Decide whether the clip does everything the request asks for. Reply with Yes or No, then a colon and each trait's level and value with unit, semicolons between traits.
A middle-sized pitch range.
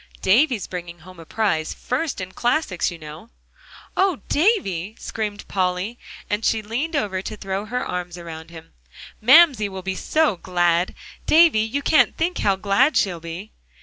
No: wide, 5.9 semitones